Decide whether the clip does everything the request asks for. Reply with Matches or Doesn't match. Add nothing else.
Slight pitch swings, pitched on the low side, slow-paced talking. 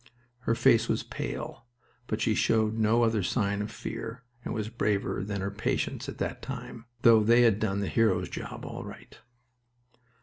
Doesn't match